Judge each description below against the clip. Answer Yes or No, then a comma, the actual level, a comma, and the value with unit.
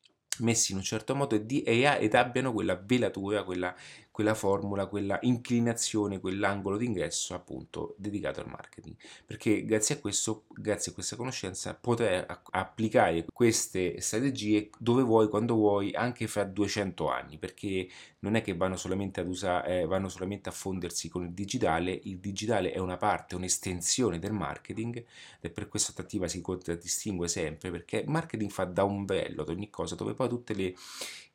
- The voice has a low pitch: Yes, low, 100 Hz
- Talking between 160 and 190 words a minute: Yes, average, 165 wpm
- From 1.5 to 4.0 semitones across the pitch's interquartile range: Yes, average, 3.2 semitones